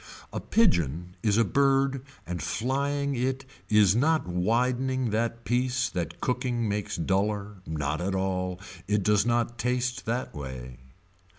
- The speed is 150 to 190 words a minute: No, slow, 135 wpm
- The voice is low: Yes, low, 110 Hz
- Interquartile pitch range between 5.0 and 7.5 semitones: Yes, wide, 5.6 semitones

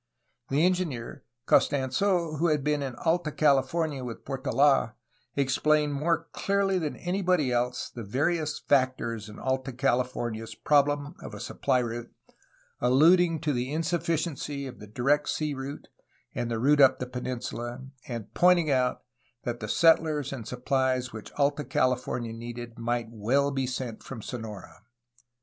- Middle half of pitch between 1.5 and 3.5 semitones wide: No, average, 3.9 semitones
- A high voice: No, low, 135 Hz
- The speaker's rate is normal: Yes, average, 145 wpm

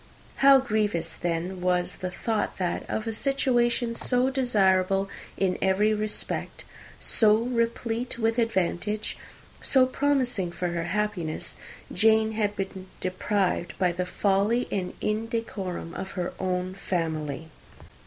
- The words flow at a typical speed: No, slow, 120 wpm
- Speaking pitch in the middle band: No, high, 205 Hz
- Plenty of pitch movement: No, average, 4.0 semitones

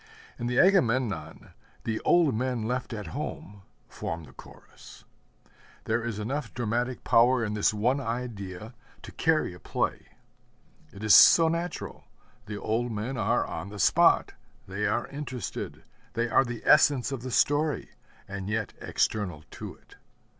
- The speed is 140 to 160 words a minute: Yes, average, 150 wpm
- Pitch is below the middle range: Yes, low, 115 Hz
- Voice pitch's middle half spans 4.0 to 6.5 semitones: No, average, 3.5 semitones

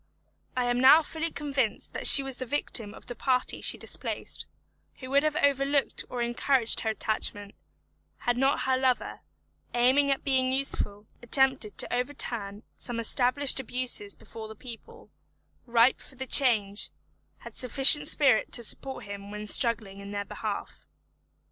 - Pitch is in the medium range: No, very high, 250 Hz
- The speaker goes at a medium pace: Yes, average, 155 wpm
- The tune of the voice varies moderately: Yes, average, 3.6 semitones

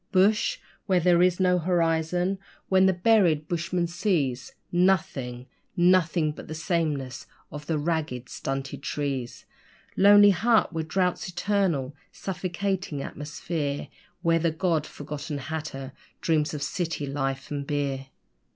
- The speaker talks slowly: Yes, slow, 125 wpm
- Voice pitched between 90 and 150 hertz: No, medium, 165 Hz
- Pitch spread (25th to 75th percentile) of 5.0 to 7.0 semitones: No, average, 4.0 semitones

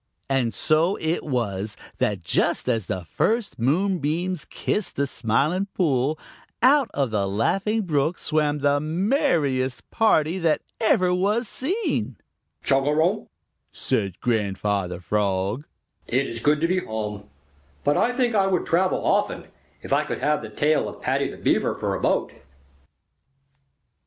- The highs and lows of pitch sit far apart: Yes, wide, 8.3 semitones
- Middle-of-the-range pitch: Yes, medium, 150 Hz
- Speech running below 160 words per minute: Yes, average, 140 wpm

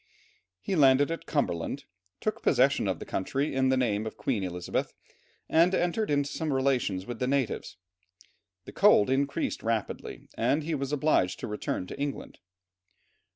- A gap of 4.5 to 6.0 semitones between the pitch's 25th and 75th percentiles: Yes, average, 4.9 semitones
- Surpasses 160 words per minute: No, average, 155 wpm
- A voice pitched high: No, low, 135 Hz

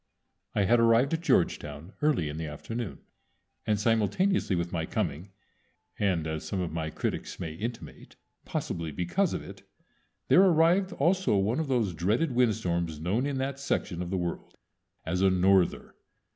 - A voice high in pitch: No, low, 100 Hz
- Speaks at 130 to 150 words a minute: No, average, 160 wpm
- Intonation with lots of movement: Yes, wide, 7.6 semitones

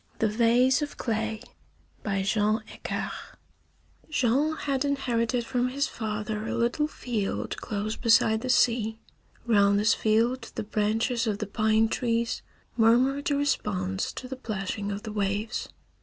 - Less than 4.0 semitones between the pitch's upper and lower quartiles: Yes, average, 2.9 semitones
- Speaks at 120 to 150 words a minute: Yes, average, 145 wpm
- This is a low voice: No, high, 225 Hz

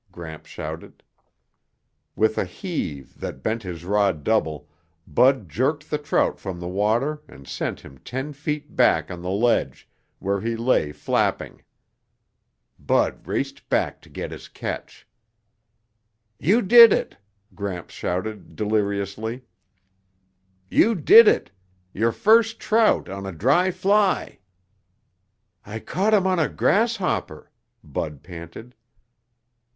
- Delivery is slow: Yes, slow, 125 wpm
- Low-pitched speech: Yes, low, 110 Hz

